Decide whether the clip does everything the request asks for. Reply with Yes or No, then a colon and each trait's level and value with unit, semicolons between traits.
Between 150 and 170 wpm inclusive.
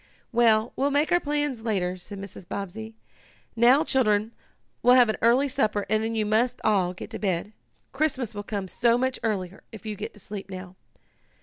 No: average, 190 wpm